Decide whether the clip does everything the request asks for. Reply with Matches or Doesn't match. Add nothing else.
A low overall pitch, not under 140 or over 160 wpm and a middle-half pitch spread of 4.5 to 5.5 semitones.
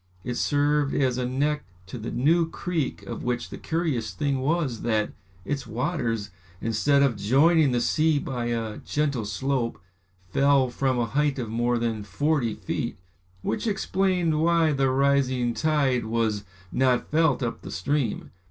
Doesn't match